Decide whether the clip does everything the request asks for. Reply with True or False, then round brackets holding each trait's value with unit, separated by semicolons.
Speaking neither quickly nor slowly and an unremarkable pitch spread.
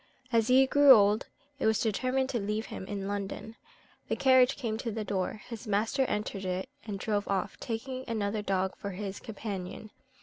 True (180 wpm; 3.1 semitones)